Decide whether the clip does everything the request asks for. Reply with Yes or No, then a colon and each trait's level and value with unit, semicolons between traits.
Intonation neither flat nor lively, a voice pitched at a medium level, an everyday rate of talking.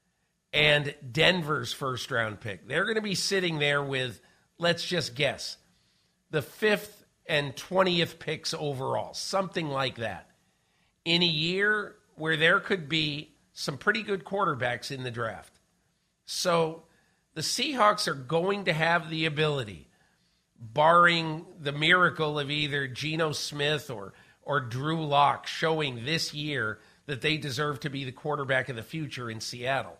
Yes: average, 3.7 semitones; medium, 155 Hz; average, 145 wpm